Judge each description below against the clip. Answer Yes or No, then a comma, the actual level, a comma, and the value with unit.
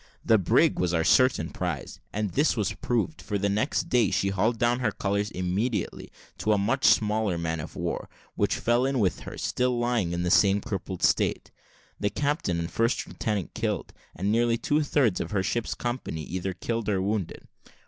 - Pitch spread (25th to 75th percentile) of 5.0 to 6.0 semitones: No, average, 4.3 semitones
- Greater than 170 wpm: Yes, average, 190 wpm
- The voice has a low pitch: Yes, low, 105 Hz